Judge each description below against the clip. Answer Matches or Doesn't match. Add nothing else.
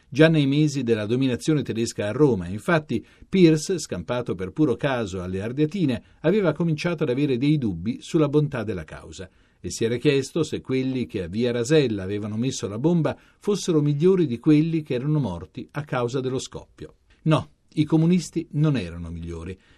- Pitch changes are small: Doesn't match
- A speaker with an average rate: Doesn't match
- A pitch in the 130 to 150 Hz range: Matches